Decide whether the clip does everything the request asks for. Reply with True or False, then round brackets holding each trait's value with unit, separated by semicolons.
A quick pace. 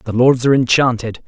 False (190 wpm)